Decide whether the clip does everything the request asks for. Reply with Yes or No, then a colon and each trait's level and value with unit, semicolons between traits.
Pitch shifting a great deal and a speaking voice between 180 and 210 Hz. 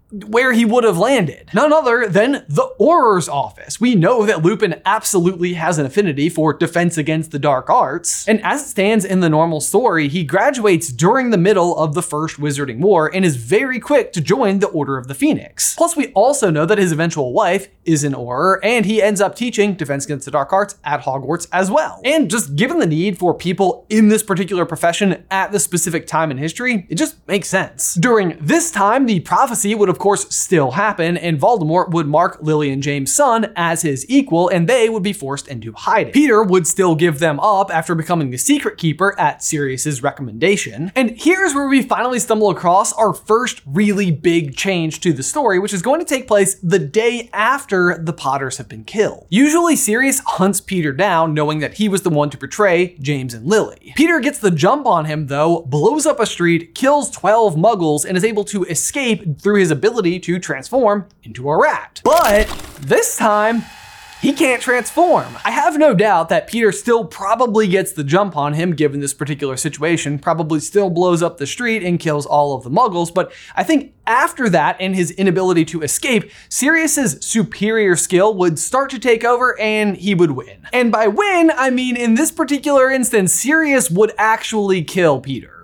Yes: wide, 5.8 semitones; high, 190 Hz